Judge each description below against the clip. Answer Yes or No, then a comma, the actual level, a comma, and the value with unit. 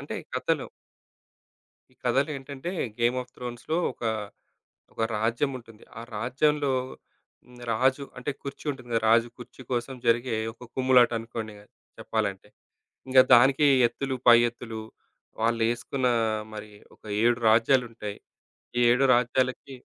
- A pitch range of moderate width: No, narrow, 2.3 semitones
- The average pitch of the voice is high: No, low, 120 Hz